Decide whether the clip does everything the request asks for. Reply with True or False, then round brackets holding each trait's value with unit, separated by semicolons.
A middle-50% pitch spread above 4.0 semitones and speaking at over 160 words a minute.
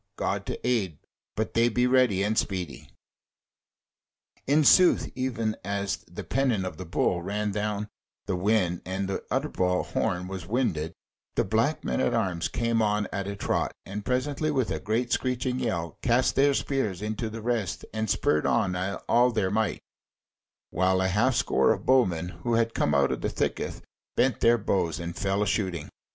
True (4.5 semitones; 175 wpm)